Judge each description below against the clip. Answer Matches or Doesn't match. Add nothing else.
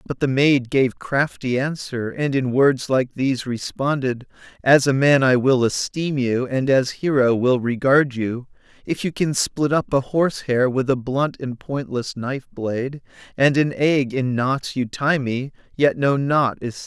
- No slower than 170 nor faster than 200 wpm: Matches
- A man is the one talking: Matches